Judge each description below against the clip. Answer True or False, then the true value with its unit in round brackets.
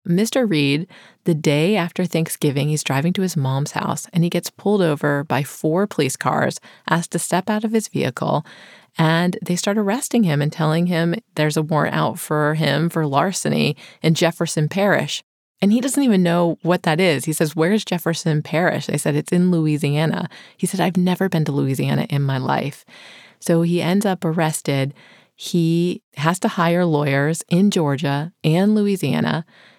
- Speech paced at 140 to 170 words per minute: False (180 wpm)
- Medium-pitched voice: True (165 Hz)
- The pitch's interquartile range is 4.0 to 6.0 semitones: False (3.3 semitones)